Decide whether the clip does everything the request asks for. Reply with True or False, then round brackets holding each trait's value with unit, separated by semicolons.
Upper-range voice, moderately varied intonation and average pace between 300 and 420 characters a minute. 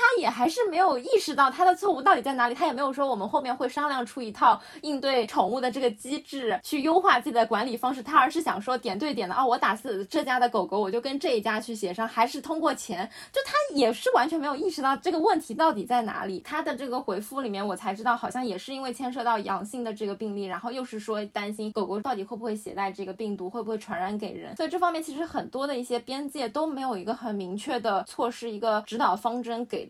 True (245 Hz; 4.8 semitones; 385 characters per minute)